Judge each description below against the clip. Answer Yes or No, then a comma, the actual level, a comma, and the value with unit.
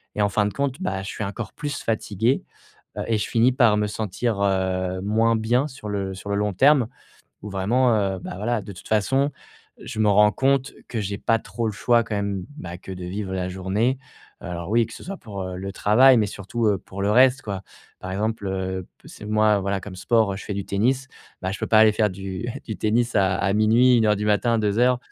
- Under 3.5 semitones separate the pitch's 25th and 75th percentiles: Yes, average, 3.1 semitones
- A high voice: No, low, 105 Hz